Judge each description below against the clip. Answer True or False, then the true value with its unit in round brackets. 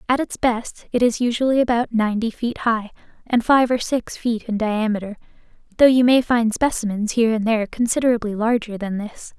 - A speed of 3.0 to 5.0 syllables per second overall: False (5.5 syllables/s)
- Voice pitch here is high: True (230 Hz)